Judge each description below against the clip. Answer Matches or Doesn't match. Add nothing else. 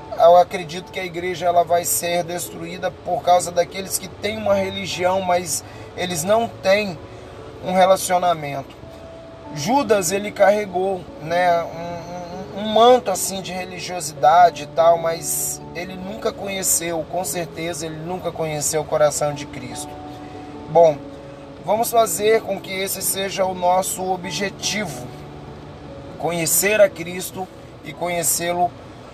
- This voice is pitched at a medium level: Matches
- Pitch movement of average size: Matches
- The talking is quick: Doesn't match